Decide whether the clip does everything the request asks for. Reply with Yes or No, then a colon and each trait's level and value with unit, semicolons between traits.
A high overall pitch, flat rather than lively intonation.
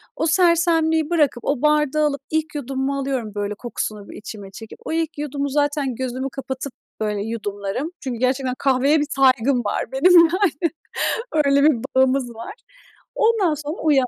No: very high, 275 Hz; average, 3.4 semitones